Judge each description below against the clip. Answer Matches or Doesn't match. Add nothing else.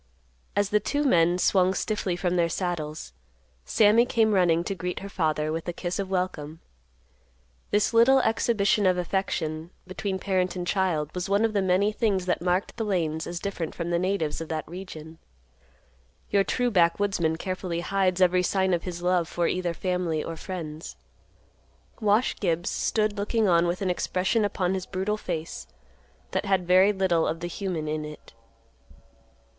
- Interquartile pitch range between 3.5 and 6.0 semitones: Doesn't match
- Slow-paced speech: Doesn't match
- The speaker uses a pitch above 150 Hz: Matches